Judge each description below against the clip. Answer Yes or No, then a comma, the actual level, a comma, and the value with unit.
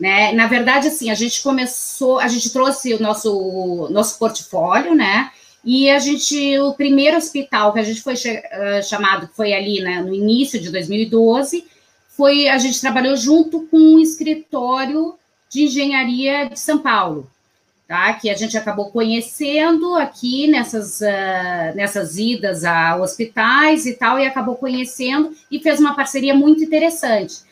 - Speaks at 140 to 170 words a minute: Yes, average, 160 wpm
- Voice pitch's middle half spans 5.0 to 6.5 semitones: Yes, average, 5.3 semitones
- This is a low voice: No, very high, 255 Hz